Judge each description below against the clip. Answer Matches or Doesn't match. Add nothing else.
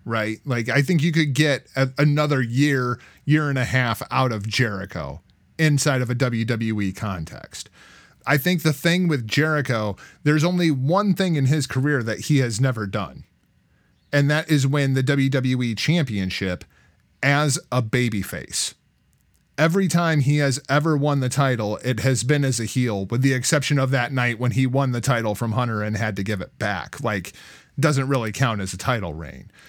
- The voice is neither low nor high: Doesn't match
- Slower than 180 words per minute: Doesn't match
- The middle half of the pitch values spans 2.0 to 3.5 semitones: Doesn't match